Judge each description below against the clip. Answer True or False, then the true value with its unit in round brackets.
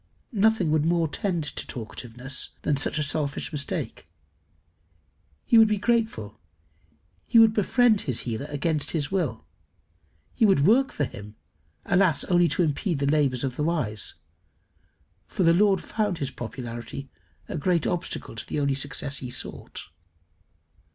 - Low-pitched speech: False (155 Hz)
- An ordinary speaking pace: True (150 wpm)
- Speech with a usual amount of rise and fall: False (5.9 semitones)